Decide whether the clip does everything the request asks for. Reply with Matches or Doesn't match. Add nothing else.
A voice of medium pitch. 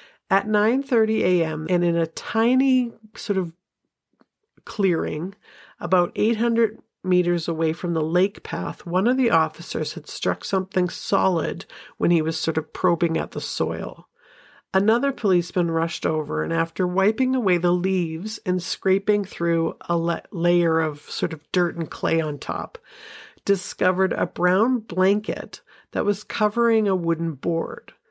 Matches